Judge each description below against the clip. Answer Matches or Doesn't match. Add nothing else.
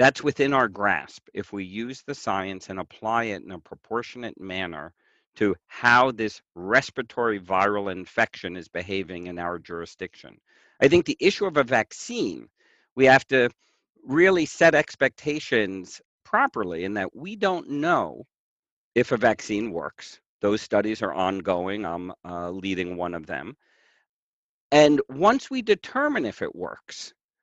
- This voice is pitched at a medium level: Doesn't match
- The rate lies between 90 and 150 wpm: Matches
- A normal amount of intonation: Doesn't match